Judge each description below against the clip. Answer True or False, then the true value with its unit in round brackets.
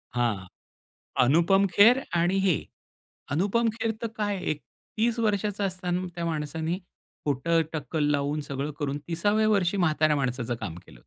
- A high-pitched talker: False (170 Hz)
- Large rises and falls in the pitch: True (5.9 semitones)